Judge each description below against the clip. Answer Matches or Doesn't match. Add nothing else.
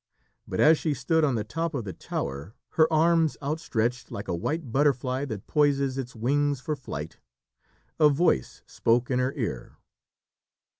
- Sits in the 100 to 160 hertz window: Matches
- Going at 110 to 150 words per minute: Doesn't match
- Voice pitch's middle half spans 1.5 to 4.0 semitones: Doesn't match